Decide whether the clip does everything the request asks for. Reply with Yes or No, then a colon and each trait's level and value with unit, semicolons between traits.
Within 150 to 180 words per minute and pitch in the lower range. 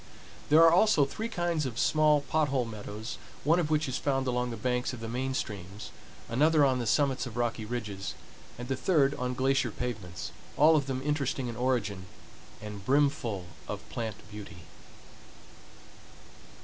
Yes: average, 165 wpm; low, 125 Hz